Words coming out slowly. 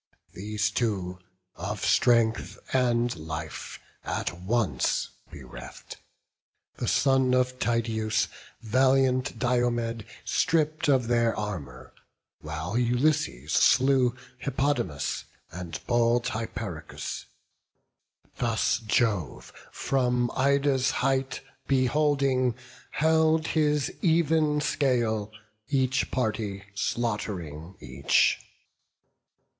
Yes: slow, 80 wpm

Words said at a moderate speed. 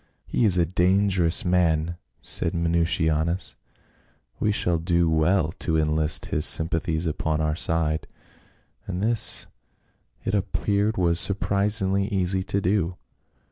No: slow, 120 wpm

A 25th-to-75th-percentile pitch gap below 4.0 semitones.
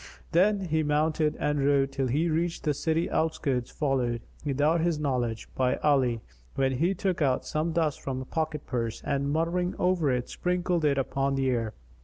Yes: average, 3.6 semitones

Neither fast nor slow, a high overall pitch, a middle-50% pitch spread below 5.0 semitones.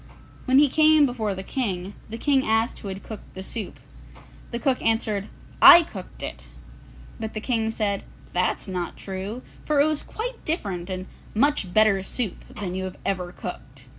No: average, 175 wpm; high, 220 Hz; wide, 5.5 semitones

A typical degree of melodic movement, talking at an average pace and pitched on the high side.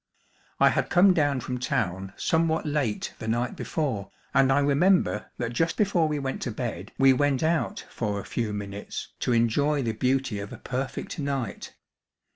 No: average, 4.8 semitones; average, 175 wpm; low, 130 Hz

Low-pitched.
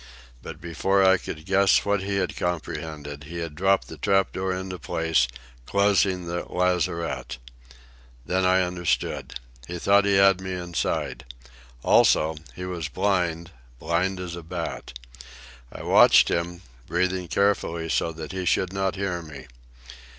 Yes: very low, 90 Hz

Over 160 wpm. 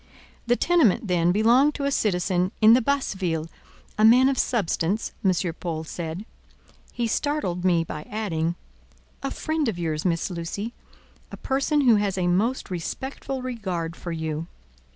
No: average, 150 wpm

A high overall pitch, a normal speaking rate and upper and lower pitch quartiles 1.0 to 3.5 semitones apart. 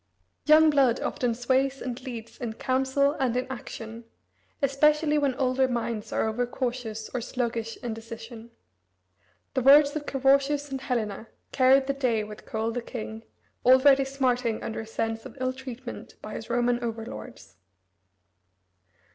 Yes: very high, 250 Hz; average, 150 wpm; average, 3.0 semitones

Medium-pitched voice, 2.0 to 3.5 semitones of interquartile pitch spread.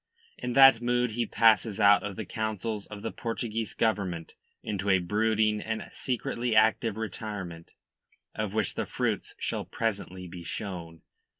No: low, 110 Hz; narrow, 2.4 semitones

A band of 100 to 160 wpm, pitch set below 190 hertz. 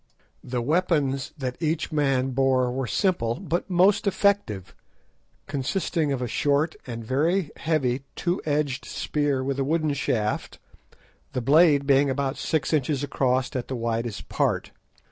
Yes: average, 145 wpm; medium, 140 Hz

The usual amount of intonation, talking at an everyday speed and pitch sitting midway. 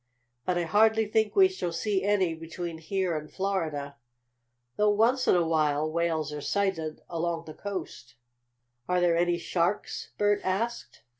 Yes: average, 4.0 semitones; average, 155 wpm; medium, 175 Hz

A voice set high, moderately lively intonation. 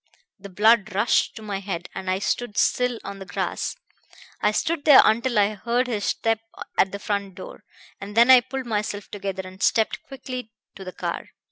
Yes: high, 210 Hz; average, 3.4 semitones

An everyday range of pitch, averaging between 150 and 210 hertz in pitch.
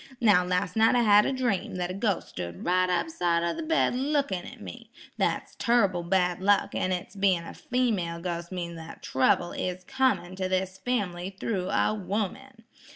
Yes: average, 4.2 semitones; high, 190 Hz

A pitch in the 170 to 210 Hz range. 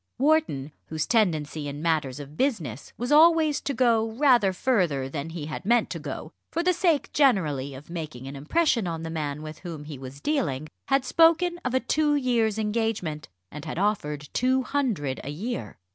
Yes: medium, 185 Hz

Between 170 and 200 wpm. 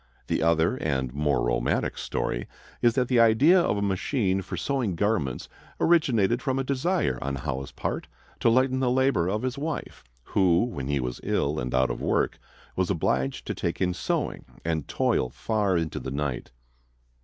Yes: average, 180 wpm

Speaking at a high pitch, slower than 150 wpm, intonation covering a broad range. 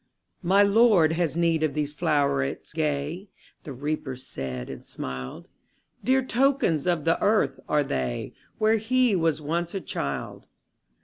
No: medium, 160 Hz; average, 140 wpm; wide, 5.9 semitones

